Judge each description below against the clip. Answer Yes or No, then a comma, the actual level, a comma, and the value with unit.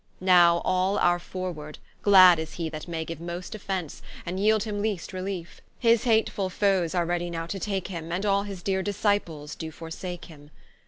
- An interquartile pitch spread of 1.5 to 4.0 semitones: Yes, average, 2.9 semitones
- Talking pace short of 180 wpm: No, average, 190 wpm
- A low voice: No, medium, 180 Hz